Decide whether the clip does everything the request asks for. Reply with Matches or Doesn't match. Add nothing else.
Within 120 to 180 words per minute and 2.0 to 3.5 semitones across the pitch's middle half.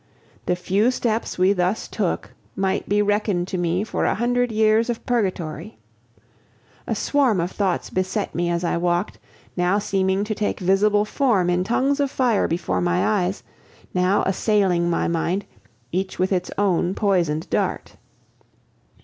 Matches